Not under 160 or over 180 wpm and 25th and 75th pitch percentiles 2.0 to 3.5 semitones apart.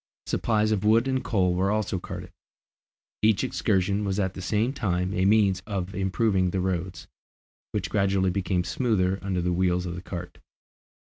Yes: average, 170 wpm; narrow, 2.5 semitones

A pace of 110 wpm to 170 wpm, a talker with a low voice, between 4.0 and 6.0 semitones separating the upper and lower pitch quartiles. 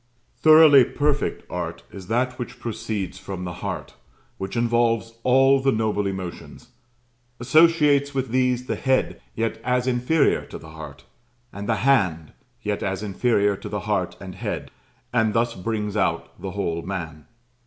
Yes: average, 155 wpm; low, 115 Hz; average, 4.8 semitones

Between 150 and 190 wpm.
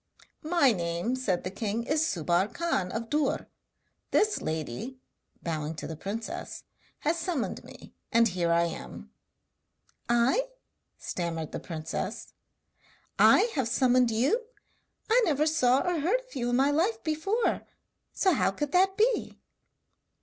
No: average, 140 wpm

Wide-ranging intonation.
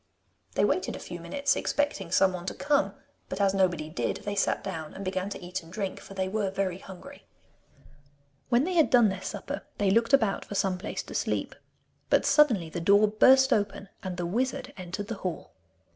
No: average, 3.8 semitones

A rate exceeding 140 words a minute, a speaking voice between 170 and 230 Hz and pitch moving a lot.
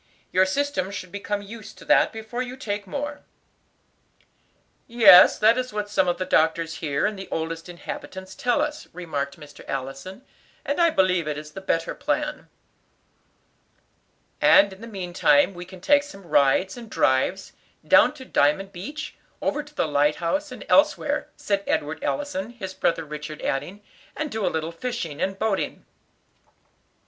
Yes: average, 160 wpm; high, 190 Hz; wide, 6.5 semitones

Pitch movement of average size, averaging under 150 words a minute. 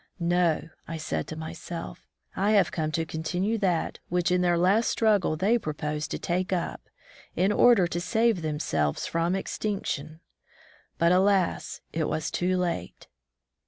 No: average, 3.3 semitones; average, 155 wpm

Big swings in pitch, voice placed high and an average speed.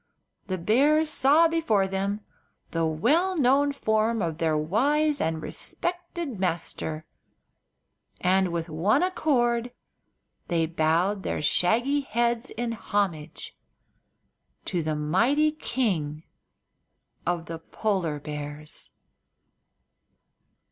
No: wide, 8.7 semitones; high, 205 Hz; slow, 100 wpm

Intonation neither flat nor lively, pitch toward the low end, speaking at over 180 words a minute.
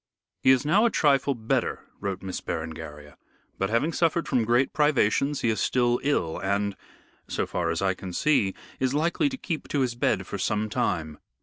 No: wide, 7.2 semitones; low, 120 Hz; average, 190 wpm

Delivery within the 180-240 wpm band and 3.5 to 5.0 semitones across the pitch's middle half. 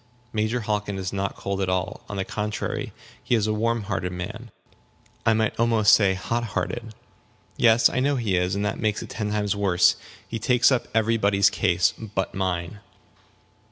No: average, 185 wpm; average, 2.8 semitones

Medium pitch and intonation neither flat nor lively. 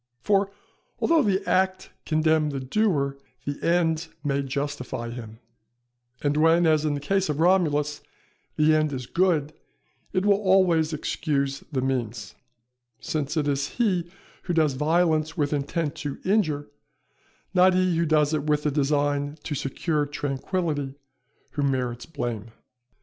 Yes: medium, 150 Hz; average, 3.4 semitones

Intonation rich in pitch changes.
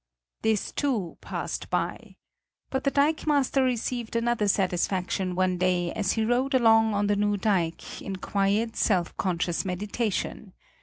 No: average, 4.2 semitones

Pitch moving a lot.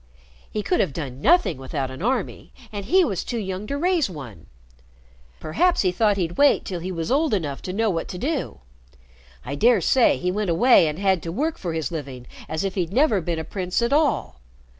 Yes: wide, 7.1 semitones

